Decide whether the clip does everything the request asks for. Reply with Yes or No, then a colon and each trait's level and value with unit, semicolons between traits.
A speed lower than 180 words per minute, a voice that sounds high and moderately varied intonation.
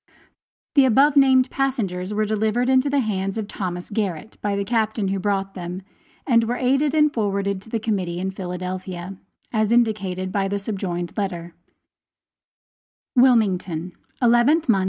Yes: average, 150 wpm; high, 205 Hz; average, 4.3 semitones